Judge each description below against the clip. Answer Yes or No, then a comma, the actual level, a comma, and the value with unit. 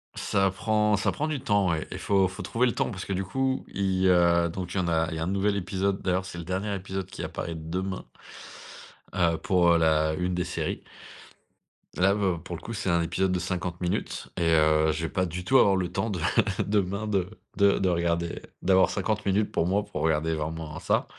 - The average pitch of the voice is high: No, very low, 95 Hz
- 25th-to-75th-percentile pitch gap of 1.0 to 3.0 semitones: Yes, narrow, 2.6 semitones